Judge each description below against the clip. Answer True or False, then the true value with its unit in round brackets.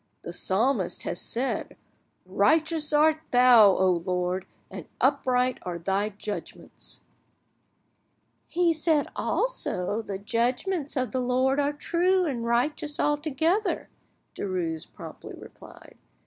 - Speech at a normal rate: False (115 wpm)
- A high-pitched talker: True (255 Hz)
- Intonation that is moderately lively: False (7.3 semitones)